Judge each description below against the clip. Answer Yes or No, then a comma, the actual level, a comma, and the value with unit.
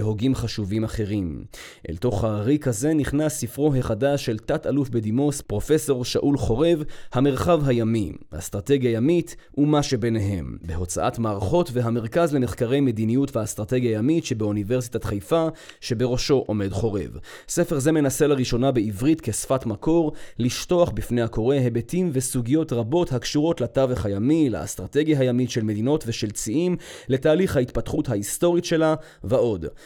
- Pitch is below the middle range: Yes, low, 125 Hz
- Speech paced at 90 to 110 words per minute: No, average, 125 wpm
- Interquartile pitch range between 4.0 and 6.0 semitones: Yes, average, 5.1 semitones